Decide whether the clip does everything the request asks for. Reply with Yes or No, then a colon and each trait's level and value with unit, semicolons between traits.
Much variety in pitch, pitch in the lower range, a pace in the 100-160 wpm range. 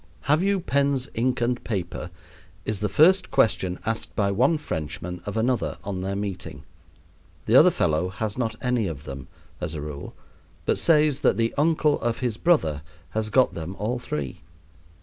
No: wide, 6.4 semitones; low, 110 Hz; average, 170 wpm